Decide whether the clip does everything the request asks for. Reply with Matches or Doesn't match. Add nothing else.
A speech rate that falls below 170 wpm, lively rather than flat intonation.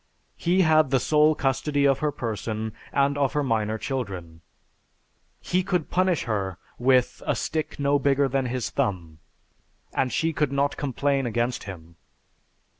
Doesn't match